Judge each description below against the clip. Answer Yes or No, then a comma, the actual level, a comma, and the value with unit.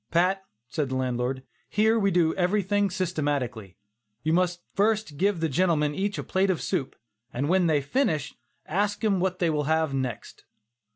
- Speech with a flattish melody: No, average, 5.0 semitones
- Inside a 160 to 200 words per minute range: Yes, average, 175 wpm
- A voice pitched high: No, medium, 170 Hz